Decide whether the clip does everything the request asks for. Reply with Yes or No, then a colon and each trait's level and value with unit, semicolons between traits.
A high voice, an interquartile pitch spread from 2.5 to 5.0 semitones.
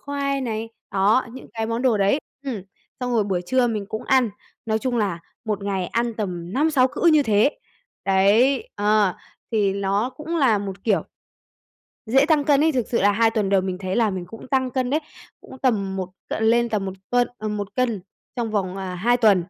Yes: high, 220 Hz; average, 4.3 semitones